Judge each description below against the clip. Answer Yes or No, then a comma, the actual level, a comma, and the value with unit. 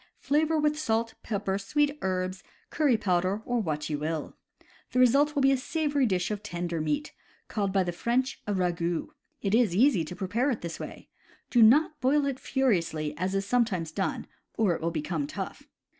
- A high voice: Yes, high, 205 Hz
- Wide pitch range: Yes, wide, 7.2 semitones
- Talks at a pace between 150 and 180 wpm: No, average, 190 wpm